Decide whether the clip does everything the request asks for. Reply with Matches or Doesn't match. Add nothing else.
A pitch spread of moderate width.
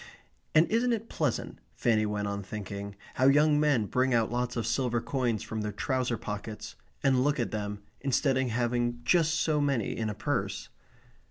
Matches